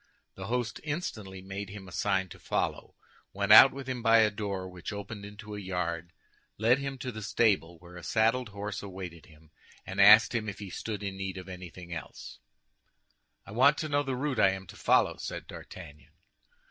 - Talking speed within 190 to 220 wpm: Yes, average, 200 wpm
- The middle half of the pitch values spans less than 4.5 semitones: Yes, average, 3.5 semitones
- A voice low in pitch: Yes, low, 100 Hz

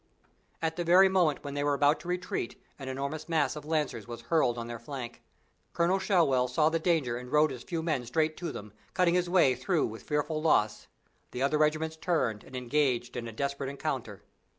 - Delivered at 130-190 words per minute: No, fast, 205 wpm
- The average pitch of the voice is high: No, medium, 145 Hz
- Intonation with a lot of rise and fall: No, average, 4.5 semitones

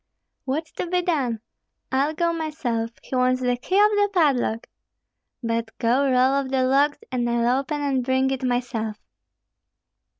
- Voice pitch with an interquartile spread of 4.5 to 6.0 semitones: No, average, 3.5 semitones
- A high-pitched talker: Yes, very high, 260 Hz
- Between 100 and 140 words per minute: No, average, 160 wpm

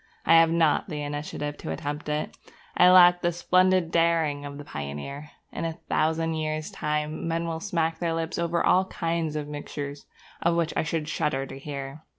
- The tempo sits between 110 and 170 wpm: No, average, 185 wpm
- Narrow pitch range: Yes, narrow, 2.3 semitones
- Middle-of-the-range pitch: Yes, medium, 160 Hz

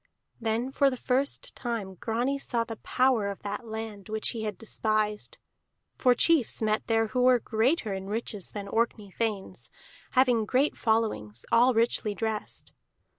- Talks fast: No, average, 155 wpm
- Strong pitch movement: No, narrow, 2.6 semitones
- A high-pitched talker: Yes, high, 225 Hz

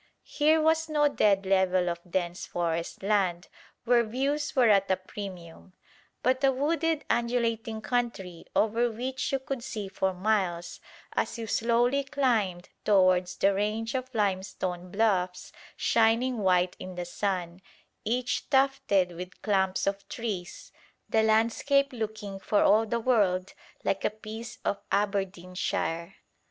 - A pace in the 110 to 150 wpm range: Yes, slow, 135 wpm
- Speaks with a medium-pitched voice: No, high, 210 Hz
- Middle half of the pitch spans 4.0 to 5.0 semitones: Yes, average, 4.7 semitones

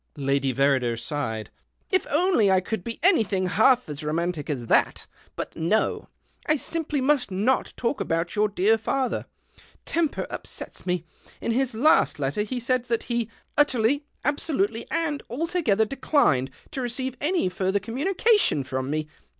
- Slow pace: No, average, 165 wpm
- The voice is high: Yes, high, 220 Hz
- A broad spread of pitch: Yes, wide, 8.5 semitones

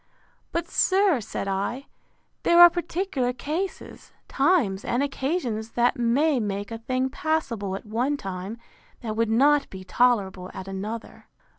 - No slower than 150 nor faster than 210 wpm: No, average, 140 wpm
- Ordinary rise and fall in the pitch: No, wide, 6.1 semitones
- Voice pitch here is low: No, high, 245 Hz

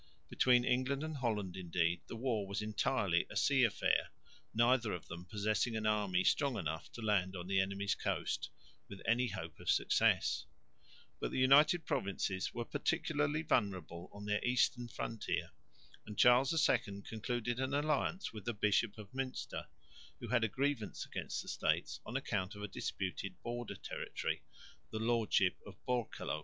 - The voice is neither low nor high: No, low, 110 Hz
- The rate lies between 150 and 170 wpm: Yes, average, 160 wpm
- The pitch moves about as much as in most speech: Yes, average, 4.2 semitones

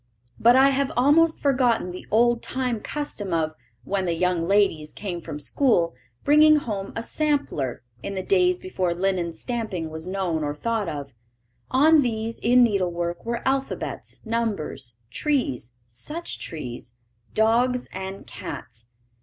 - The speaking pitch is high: Yes, high, 205 Hz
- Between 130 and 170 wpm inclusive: Yes, average, 140 wpm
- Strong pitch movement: Yes, wide, 7.2 semitones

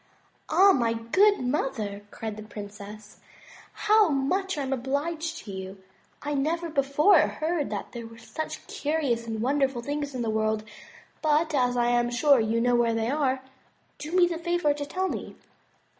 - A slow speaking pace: No, average, 175 wpm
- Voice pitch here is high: Yes, very high, 270 Hz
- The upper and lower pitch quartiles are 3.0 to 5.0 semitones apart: No, wide, 5.4 semitones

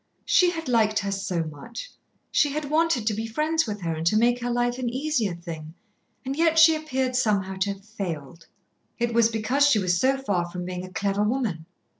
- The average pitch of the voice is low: No, high, 220 Hz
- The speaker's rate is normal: No, fast, 210 wpm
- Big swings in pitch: Yes, wide, 6.2 semitones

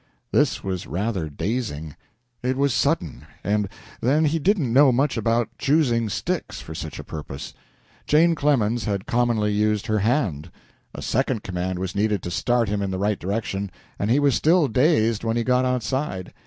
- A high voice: No, low, 110 Hz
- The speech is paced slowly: No, average, 180 wpm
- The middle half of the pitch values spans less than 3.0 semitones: No, average, 4.9 semitones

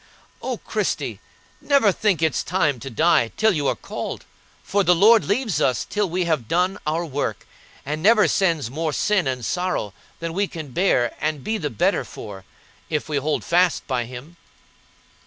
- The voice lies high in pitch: No, medium, 165 Hz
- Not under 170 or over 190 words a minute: Yes, average, 175 wpm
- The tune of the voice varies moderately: No, wide, 5.7 semitones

